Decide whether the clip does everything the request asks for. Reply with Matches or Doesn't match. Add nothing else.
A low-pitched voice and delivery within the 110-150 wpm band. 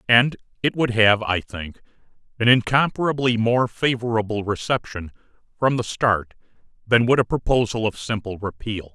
Matches